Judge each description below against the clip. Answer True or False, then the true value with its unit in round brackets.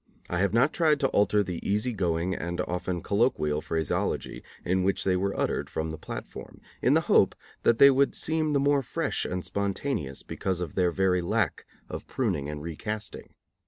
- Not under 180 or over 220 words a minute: True (185 wpm)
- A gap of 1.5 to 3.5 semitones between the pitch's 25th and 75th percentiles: False (5.1 semitones)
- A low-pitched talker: True (95 Hz)